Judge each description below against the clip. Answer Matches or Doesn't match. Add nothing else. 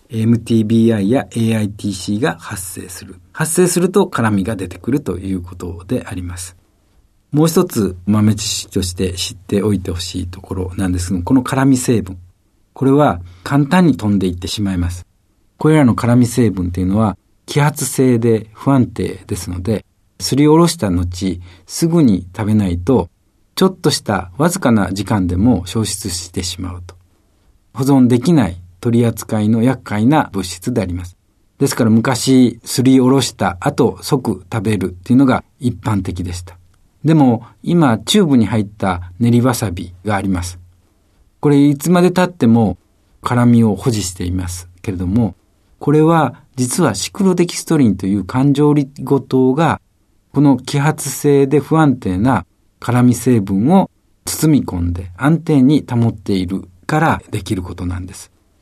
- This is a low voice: Matches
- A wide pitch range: Matches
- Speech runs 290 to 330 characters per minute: Matches